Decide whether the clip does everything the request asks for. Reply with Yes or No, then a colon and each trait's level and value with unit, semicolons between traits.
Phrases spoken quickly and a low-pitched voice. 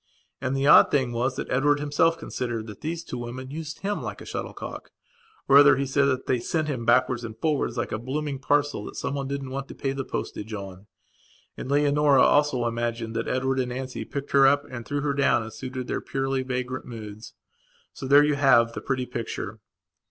Yes: fast, 210 wpm; low, 130 Hz